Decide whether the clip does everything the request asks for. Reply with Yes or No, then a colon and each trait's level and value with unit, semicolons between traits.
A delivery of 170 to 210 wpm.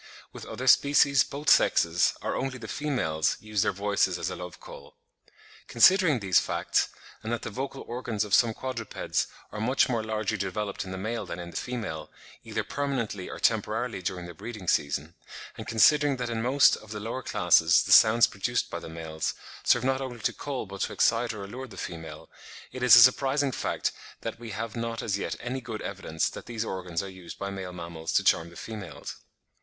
Yes: fast, 205 wpm